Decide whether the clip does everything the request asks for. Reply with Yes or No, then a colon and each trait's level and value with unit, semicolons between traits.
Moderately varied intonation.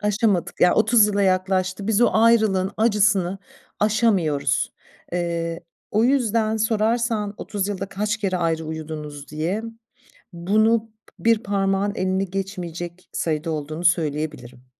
Yes: average, 4.1 semitones